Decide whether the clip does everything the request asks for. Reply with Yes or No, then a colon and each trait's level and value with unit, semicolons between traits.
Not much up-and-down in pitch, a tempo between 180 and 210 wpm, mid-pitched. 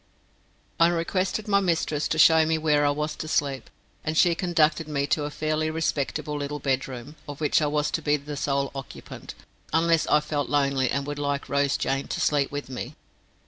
Yes: narrow, 2.0 semitones; average, 190 wpm; medium, 150 Hz